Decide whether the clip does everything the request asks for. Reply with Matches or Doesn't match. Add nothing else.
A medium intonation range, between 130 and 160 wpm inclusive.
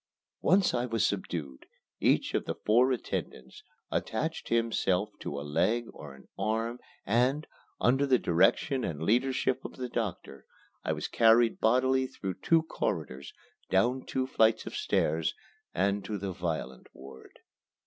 Doesn't match